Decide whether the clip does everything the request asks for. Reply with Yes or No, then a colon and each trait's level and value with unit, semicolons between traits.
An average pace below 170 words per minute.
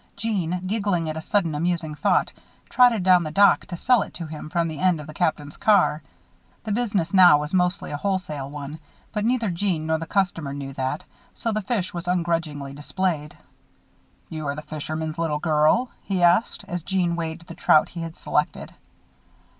No: average, 185 wpm